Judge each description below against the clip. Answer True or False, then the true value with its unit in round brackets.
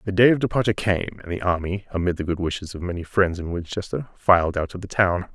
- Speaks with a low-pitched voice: True (95 Hz)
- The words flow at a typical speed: False (245 wpm)